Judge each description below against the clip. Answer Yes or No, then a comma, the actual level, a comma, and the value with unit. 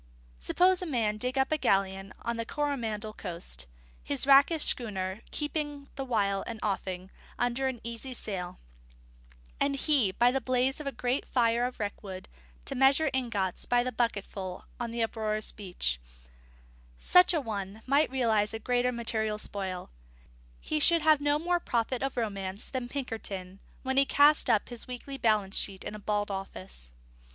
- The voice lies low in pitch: No, high, 235 Hz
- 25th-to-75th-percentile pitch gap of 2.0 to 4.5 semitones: No, average, 5.1 semitones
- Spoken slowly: No, average, 165 wpm